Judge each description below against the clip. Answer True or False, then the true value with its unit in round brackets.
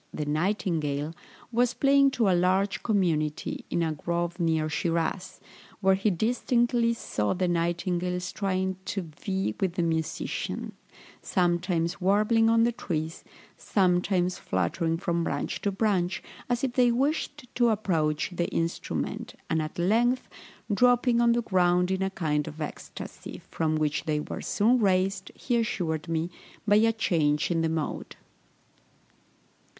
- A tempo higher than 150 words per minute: False (145 wpm)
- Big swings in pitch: False (4.8 semitones)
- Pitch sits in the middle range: True (180 Hz)